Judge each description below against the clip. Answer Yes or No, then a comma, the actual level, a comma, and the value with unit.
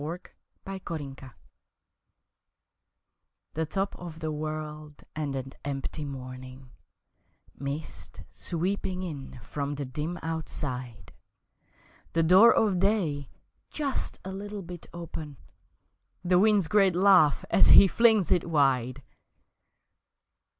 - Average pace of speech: No, slow, 110 wpm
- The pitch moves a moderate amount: Yes, average, 4.8 semitones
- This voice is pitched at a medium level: Yes, medium, 160 Hz